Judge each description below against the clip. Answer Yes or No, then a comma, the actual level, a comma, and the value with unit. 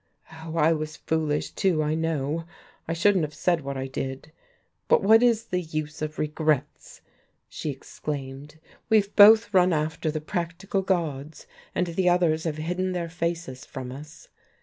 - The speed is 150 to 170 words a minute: Yes, average, 160 wpm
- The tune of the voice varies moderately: Yes, average, 3.0 semitones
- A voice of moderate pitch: Yes, medium, 160 Hz